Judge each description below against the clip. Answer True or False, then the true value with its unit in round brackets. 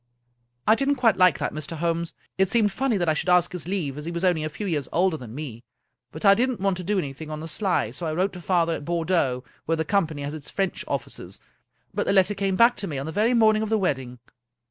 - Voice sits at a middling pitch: True (175 Hz)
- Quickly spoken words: True (265 wpm)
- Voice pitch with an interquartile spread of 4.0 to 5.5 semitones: True (4.3 semitones)